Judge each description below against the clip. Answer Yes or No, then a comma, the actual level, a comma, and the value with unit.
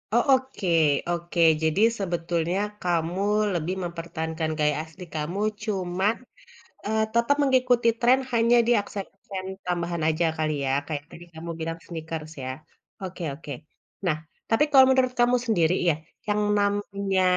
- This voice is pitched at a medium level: Yes, medium, 180 Hz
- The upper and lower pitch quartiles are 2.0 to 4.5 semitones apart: No, average, 4.9 semitones